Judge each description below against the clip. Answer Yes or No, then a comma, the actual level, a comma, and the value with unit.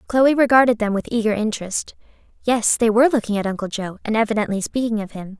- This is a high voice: Yes, high, 220 Hz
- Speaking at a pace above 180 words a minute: Yes, average, 200 wpm